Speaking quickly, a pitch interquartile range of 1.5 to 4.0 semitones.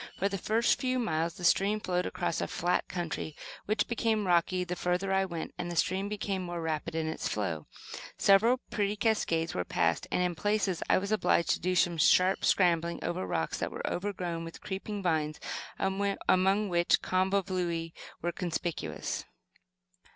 No: average, 170 wpm; average, 2.9 semitones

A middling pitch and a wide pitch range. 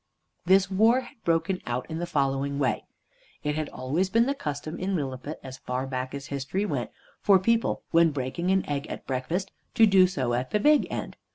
Yes: medium, 160 Hz; wide, 6.1 semitones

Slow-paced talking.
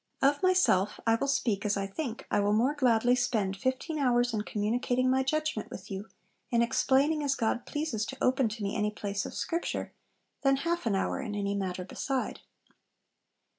No: average, 185 wpm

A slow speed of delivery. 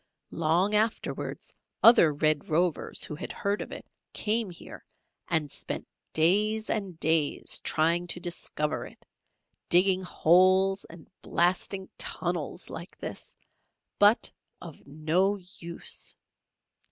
Yes: slow, 115 wpm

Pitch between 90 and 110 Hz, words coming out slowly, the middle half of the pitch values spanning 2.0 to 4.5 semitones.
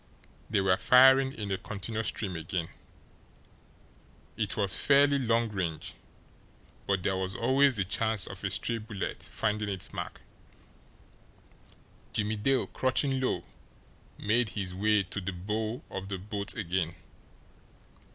Yes: low, 105 Hz; slow, 130 wpm; average, 3.4 semitones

